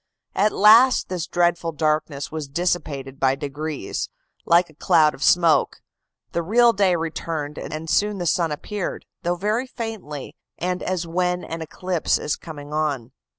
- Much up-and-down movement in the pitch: No, average, 3.2 semitones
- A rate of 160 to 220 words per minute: No, average, 150 wpm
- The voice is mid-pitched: Yes, medium, 165 Hz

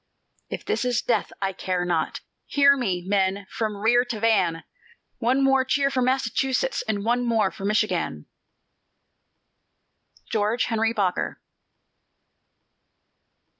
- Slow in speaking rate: Yes, slow, 120 wpm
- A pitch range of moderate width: Yes, average, 4.1 semitones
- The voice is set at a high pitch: Yes, high, 225 Hz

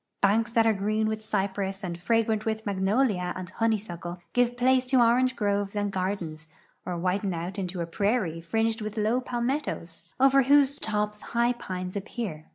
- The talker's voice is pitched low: No, high, 210 Hz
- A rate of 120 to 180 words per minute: Yes, average, 165 wpm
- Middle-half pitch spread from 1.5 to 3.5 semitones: No, average, 4.0 semitones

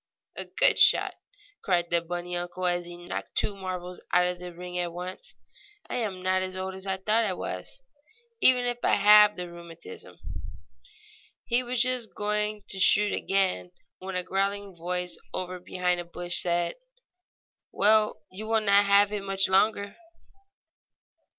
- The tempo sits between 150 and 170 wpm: Yes, average, 165 wpm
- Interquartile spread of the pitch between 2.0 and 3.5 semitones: Yes, average, 2.7 semitones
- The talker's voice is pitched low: No, medium, 185 Hz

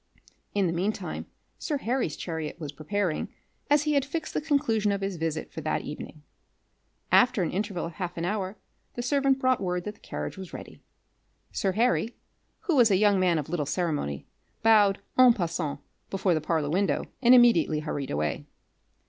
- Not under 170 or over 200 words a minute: Yes, average, 180 wpm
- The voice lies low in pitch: No, high, 190 Hz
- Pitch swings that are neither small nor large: No, wide, 6.4 semitones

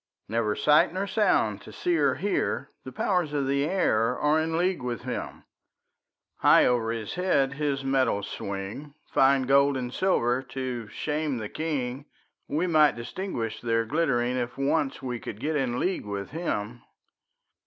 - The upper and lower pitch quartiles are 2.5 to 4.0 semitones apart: No, average, 4.4 semitones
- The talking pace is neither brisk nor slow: Yes, average, 160 wpm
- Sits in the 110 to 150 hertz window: Yes, low, 135 Hz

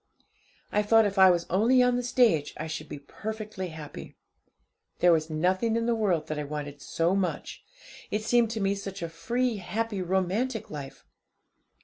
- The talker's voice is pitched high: Yes, high, 195 Hz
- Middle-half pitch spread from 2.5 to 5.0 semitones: No, wide, 5.6 semitones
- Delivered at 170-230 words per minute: Yes, average, 175 wpm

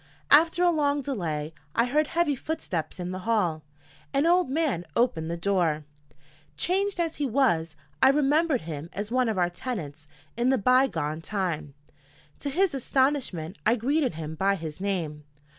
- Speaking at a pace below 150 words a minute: No, average, 165 wpm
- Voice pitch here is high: Yes, high, 225 Hz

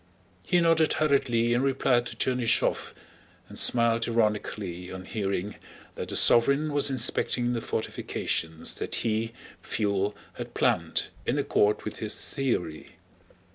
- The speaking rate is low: Yes, slow, 130 wpm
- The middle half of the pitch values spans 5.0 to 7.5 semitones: No, average, 4.0 semitones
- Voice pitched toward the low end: Yes, low, 115 Hz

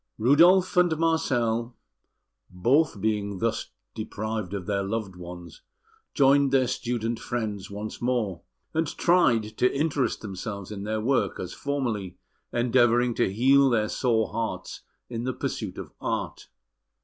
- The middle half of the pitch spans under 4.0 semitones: No, average, 4.3 semitones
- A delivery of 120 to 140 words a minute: Yes, slow, 135 wpm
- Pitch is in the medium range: No, low, 115 Hz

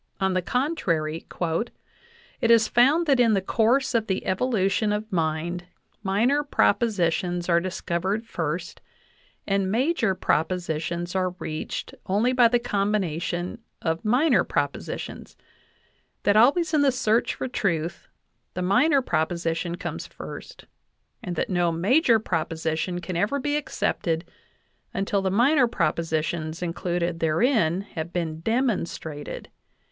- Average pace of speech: No, slow, 125 wpm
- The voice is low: No, high, 190 Hz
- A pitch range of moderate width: No, wide, 5.8 semitones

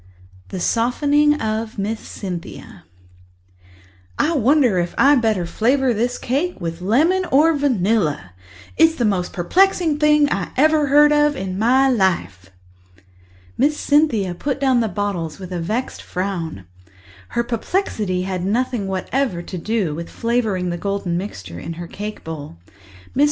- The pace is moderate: Yes, average, 145 wpm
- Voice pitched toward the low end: No, high, 220 Hz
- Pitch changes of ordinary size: No, wide, 7.4 semitones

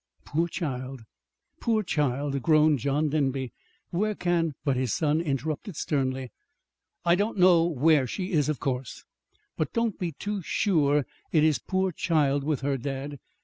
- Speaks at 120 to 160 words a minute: Yes, average, 155 wpm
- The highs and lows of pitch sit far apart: No, average, 3.9 semitones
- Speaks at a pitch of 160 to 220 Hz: No, medium, 150 Hz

